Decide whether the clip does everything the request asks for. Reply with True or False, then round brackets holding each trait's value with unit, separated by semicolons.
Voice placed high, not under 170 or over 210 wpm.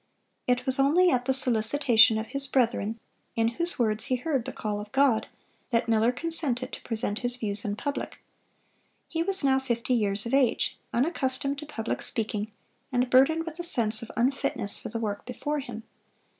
True (245 Hz; 185 wpm)